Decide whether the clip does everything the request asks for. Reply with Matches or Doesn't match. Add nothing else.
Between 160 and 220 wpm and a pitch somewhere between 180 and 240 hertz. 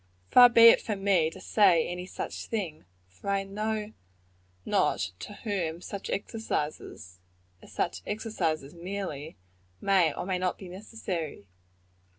Doesn't match